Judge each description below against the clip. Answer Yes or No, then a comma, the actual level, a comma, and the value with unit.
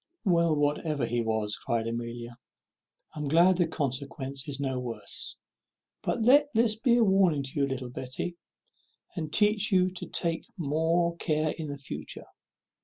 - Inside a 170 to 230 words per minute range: No, average, 160 wpm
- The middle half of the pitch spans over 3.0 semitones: Yes, average, 5.2 semitones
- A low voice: No, medium, 150 Hz